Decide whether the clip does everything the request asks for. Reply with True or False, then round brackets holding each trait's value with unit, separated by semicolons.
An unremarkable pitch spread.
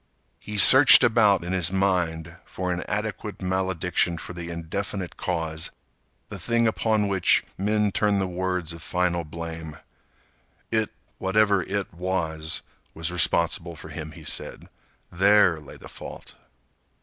True (3.2 semitones)